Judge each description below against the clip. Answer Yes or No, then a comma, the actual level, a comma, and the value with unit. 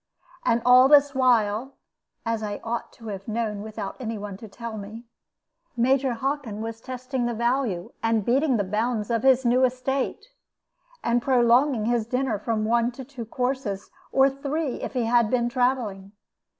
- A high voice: Yes, high, 235 Hz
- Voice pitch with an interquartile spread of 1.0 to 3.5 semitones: Yes, average, 2.9 semitones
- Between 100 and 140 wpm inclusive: No, average, 165 wpm